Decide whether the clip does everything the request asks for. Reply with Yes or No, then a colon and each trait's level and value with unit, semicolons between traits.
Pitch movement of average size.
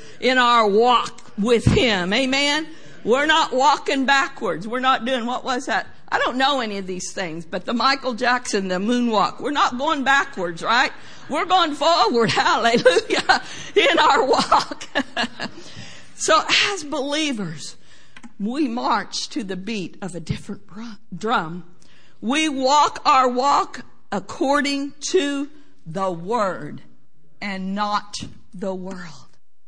No: wide, 6.2 semitones